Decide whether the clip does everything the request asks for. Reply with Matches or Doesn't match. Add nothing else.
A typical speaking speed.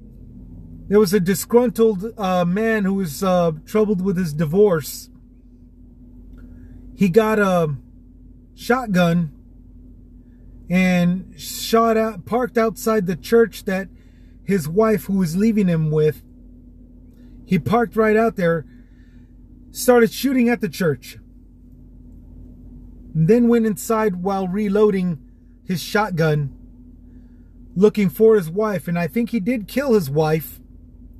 Doesn't match